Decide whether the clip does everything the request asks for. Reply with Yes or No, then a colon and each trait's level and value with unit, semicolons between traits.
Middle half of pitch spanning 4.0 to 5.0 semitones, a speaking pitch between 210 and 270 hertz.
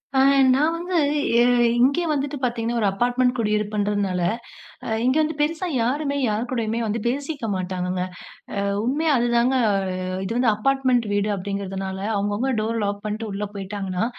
Yes: average, 4.7 semitones; high, 230 Hz